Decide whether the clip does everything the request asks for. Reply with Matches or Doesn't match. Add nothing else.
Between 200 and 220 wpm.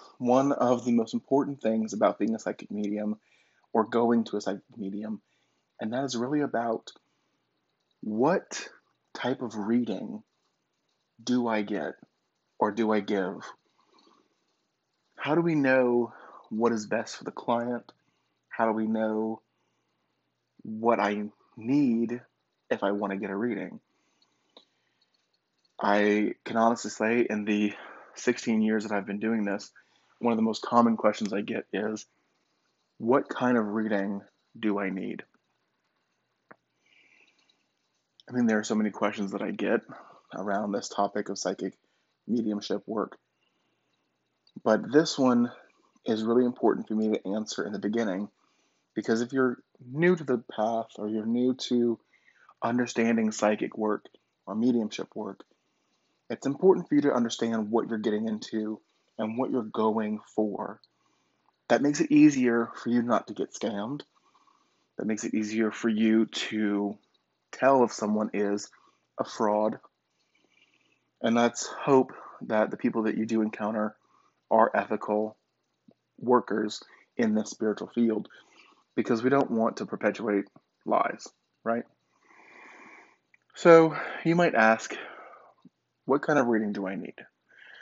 Doesn't match